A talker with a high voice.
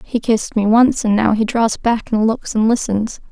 Yes: high, 225 Hz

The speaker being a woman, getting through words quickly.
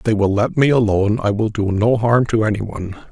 No: male; fast, 270 wpm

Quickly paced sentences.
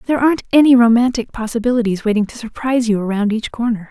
No: average, 185 wpm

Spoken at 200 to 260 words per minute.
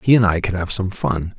No: fast, 305 wpm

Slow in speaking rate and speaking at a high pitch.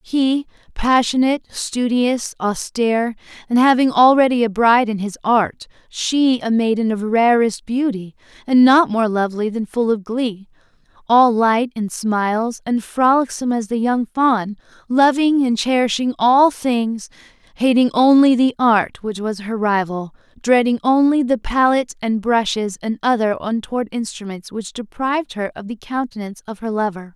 No: average, 150 wpm; high, 235 Hz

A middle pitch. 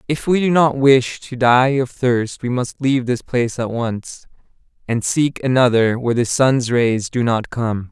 No: low, 125 Hz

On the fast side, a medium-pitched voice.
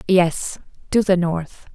No: slow, 135 wpm; medium, 180 Hz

